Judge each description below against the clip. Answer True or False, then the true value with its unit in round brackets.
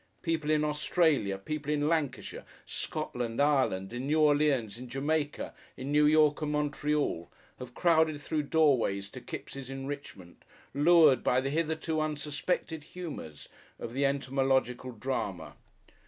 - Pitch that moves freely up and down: False (3.2 semitones)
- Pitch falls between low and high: True (145 Hz)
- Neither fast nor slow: False (130 wpm)